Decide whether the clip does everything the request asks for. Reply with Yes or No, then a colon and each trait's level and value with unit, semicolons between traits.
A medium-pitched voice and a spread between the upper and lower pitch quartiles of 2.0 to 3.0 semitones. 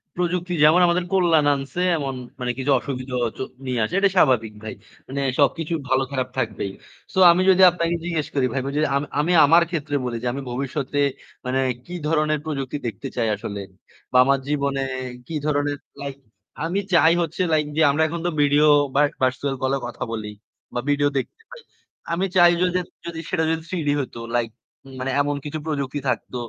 No: medium, 145 Hz; average, 3.9 semitones